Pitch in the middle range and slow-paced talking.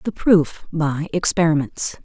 Yes: medium, 160 Hz; slow, 120 wpm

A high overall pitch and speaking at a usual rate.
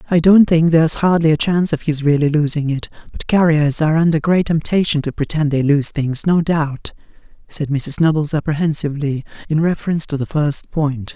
No: medium, 155 Hz; average, 190 wpm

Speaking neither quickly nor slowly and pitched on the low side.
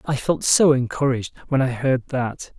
Yes: average, 185 wpm; low, 130 Hz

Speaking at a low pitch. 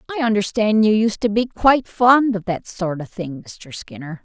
No: high, 215 Hz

